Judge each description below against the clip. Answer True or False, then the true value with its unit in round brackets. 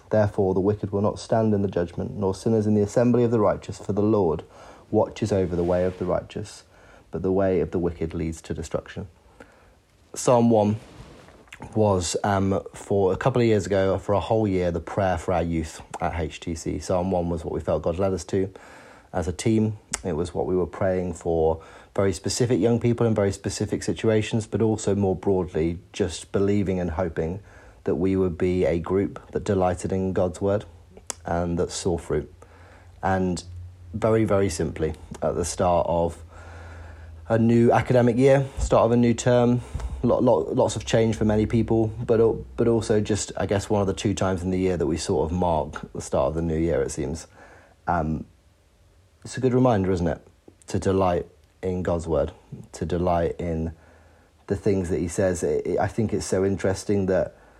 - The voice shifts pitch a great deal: False (3.4 semitones)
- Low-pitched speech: True (95 Hz)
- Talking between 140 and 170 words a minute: False (190 wpm)